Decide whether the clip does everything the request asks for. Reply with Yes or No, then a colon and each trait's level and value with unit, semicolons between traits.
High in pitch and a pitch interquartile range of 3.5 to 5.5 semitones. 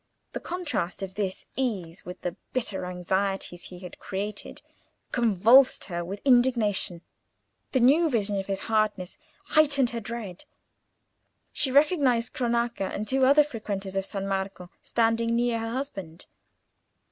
Yes: high, 215 Hz; average, 4.6 semitones